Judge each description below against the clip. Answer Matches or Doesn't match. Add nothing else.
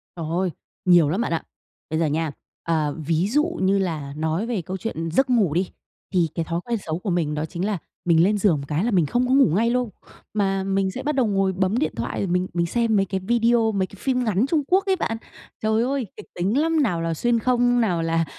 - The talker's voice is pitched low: Doesn't match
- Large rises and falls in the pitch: Matches